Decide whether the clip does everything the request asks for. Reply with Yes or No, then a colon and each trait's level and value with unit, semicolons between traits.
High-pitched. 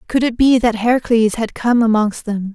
Yes: high, 225 Hz